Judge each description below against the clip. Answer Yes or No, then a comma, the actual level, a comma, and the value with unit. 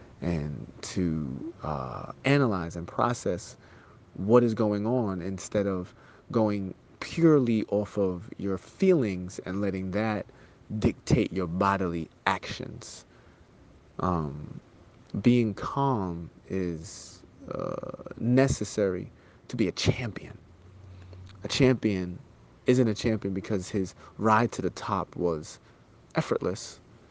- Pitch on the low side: Yes, low, 100 Hz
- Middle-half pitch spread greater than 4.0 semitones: Yes, average, 4.6 semitones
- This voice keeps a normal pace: No, slow, 105 wpm